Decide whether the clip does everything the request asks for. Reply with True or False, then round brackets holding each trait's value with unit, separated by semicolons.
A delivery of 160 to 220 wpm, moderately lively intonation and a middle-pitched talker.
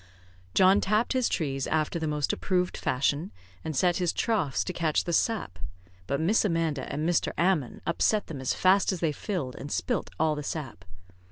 True (185 wpm; 4.2 semitones; 165 Hz)